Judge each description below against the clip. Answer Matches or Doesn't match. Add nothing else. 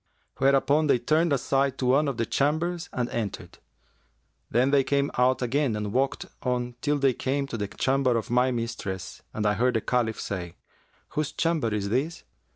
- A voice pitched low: Matches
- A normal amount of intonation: Matches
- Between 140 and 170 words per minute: Doesn't match